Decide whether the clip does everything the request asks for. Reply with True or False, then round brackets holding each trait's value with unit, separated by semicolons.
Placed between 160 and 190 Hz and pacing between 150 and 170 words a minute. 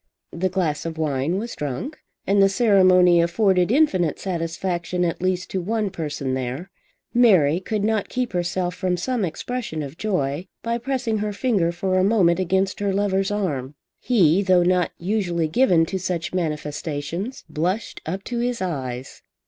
True (185 Hz; 160 wpm)